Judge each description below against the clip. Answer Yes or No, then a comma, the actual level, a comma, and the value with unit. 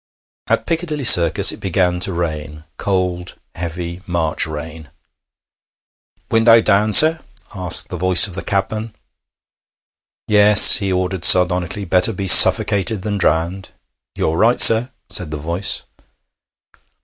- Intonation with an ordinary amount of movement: Yes, average, 3.3 semitones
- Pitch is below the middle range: Yes, very low, 95 Hz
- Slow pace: Yes, slow, 125 wpm